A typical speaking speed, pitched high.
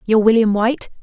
Yes: average, 175 wpm; high, 220 Hz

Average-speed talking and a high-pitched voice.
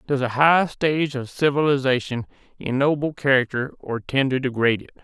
No: average, 155 wpm; low, 135 Hz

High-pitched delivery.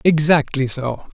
No: medium, 145 Hz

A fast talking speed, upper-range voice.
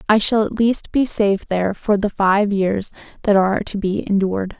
Yes: fast, 210 wpm; high, 205 Hz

